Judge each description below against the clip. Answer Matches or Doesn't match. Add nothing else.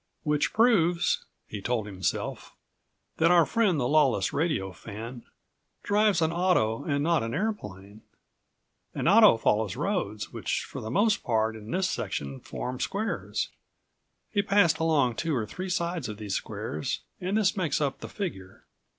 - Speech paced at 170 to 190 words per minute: Doesn't match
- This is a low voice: Doesn't match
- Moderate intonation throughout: Doesn't match